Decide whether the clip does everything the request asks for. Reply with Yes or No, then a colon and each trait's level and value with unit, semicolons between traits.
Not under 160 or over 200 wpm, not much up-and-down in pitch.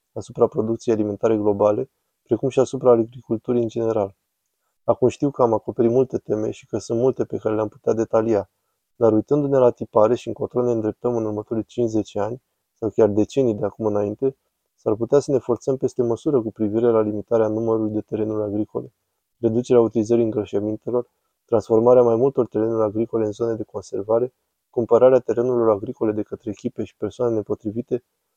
Yes: fast, 170 wpm; narrow, 2.1 semitones